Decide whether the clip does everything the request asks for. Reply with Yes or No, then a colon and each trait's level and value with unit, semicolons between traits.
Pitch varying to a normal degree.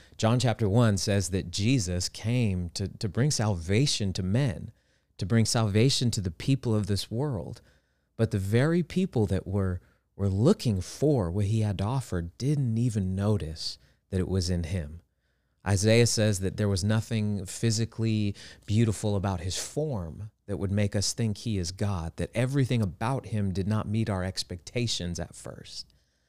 Yes: average, 3.4 semitones